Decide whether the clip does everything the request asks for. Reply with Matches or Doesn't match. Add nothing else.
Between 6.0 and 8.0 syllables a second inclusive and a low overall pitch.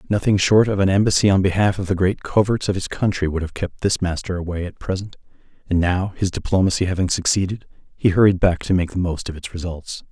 Matches